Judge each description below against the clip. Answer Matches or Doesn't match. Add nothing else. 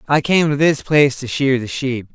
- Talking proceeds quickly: Matches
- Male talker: Matches